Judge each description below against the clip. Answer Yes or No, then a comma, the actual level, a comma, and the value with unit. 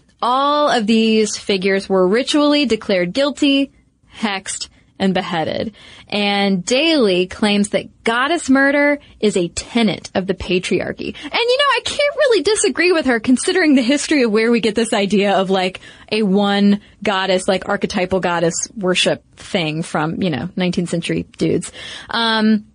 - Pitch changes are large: Yes, wide, 6.1 semitones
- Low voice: No, high, 215 Hz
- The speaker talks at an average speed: Yes, average, 155 wpm